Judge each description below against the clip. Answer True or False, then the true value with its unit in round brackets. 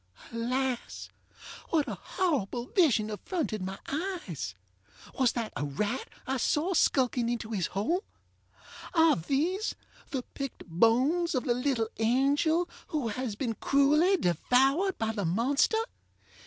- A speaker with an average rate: False (130 wpm)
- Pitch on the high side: True (255 Hz)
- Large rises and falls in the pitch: True (5.7 semitones)